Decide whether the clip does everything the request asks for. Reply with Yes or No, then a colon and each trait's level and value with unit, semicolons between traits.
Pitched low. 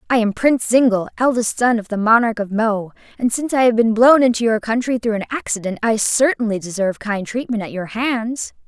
No: high, 225 Hz